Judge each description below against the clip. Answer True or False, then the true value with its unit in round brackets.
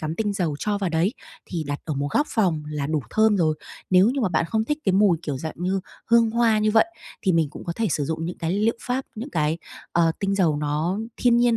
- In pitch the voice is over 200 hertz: False (185 Hz)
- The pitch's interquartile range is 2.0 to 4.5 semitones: False (5.6 semitones)